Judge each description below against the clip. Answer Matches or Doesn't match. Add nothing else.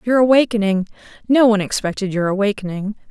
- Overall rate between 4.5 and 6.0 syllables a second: Doesn't match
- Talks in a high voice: Matches